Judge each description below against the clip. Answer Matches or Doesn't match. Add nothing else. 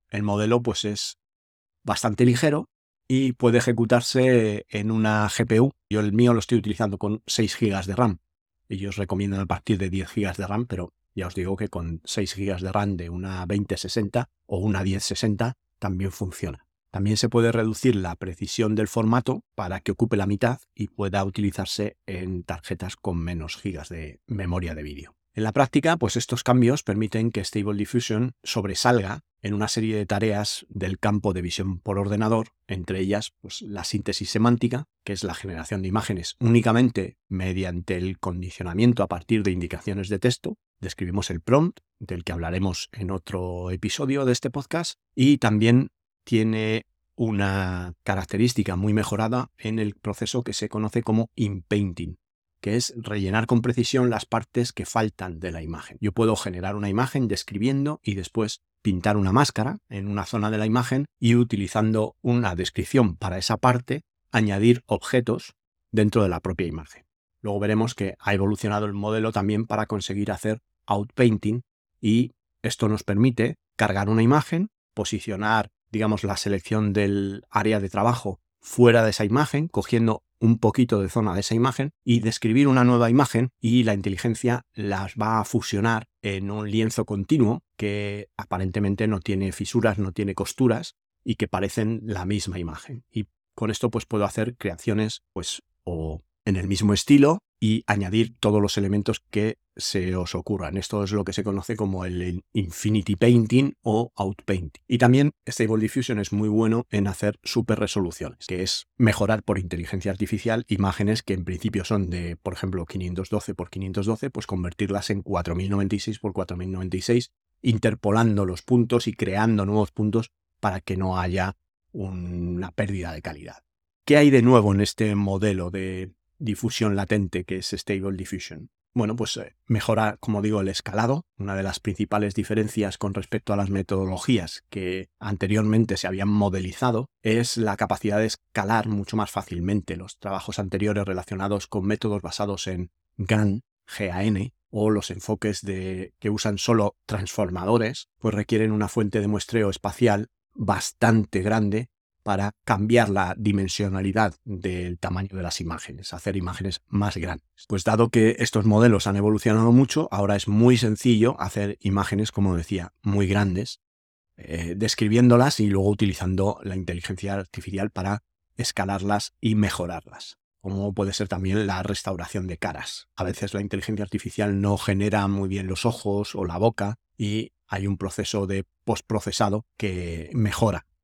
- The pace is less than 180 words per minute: Matches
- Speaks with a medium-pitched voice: Doesn't match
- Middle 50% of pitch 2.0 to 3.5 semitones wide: Matches